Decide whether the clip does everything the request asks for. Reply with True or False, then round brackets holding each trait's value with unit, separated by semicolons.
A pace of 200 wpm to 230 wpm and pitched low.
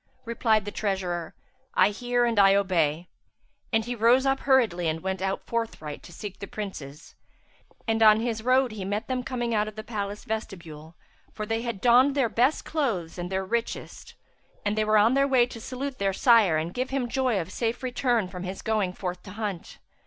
False (205 wpm; 215 Hz)